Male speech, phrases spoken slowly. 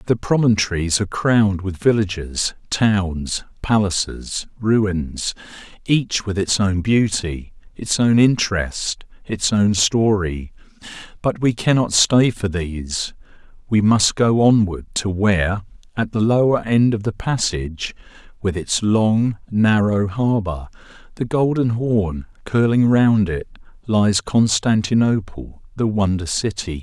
Yes: male; slow, 125 wpm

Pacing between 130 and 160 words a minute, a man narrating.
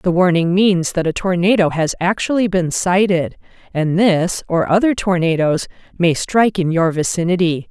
No: average, 155 wpm; female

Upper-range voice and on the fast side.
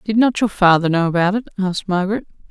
Yes: high, 195 Hz; fast, 215 wpm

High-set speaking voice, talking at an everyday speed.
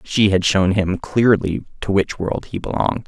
No: low, 100 Hz; average, 195 wpm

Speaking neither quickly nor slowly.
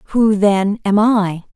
Yes: average, 155 wpm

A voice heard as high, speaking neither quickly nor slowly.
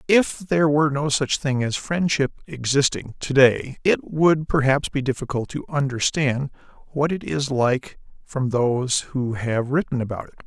No: medium, 140 Hz; average, 165 wpm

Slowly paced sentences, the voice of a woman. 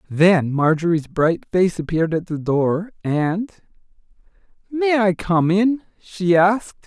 No: slow, 130 wpm; male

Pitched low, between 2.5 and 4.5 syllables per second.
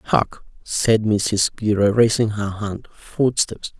Yes: low, 105 Hz; 3.2 syllables/s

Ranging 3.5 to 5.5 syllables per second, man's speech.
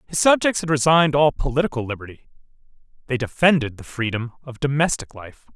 No: 6.1 syllables/s; male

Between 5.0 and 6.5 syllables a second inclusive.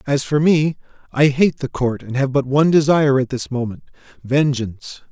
Yes: 5.3 syllables/s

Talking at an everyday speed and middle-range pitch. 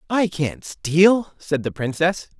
Yes: average, 150 wpm; medium, 170 Hz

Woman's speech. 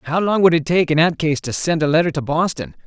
No: male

